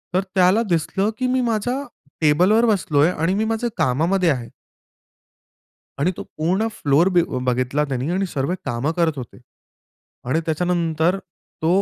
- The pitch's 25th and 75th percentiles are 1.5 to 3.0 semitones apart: No, average, 4.8 semitones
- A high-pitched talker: No, medium, 170 Hz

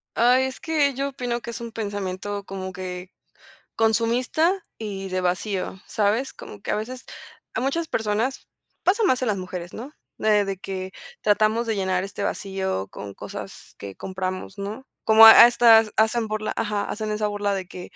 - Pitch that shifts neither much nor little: Yes, average, 3.8 semitones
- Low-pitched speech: No, high, 215 Hz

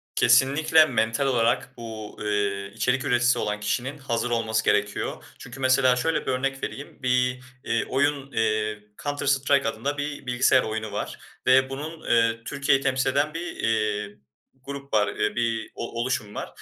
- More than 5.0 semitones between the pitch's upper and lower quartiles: No, average, 3.6 semitones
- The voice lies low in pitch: Yes, low, 125 Hz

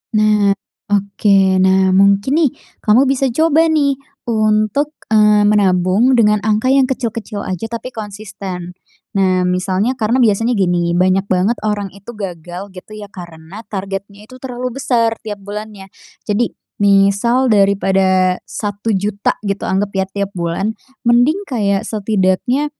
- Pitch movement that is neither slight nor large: Yes, average, 3.2 semitones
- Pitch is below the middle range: No, high, 205 Hz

